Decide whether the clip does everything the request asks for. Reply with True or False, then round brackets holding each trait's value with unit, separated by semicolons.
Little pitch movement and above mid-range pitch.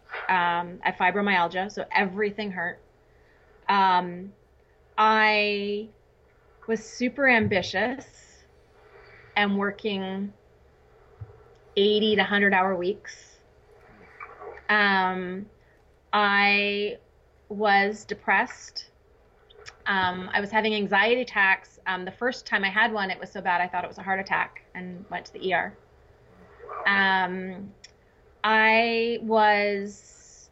True (2.3 semitones; 200 Hz)